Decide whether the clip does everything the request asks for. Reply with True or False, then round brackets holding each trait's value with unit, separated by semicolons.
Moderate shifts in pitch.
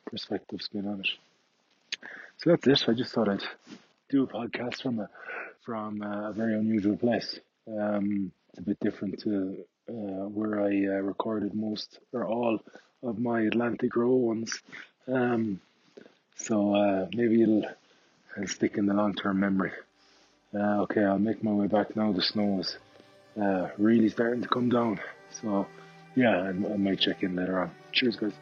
False (2.2 semitones)